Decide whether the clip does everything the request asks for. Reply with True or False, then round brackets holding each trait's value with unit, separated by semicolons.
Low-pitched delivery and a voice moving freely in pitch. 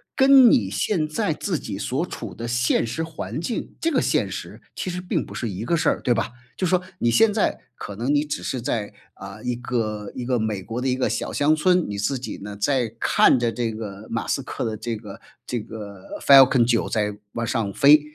True (120 Hz; 5.7 semitones)